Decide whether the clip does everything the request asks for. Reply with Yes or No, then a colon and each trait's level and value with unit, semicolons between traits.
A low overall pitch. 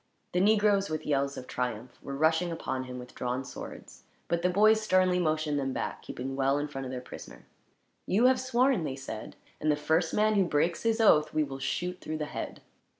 No: medium, 155 Hz